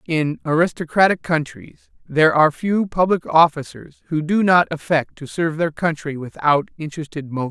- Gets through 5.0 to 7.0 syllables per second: Yes, 5.4 syllables/s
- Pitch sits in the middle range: Yes, medium, 160 Hz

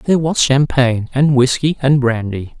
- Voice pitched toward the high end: No, low, 135 Hz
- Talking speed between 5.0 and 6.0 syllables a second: No, 4.8 syllables/s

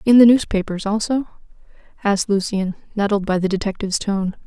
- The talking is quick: No, average, 150 wpm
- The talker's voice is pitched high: Yes, high, 205 Hz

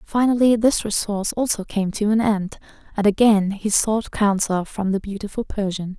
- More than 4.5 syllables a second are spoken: Yes, 4.9 syllables/s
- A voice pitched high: Yes, high, 210 Hz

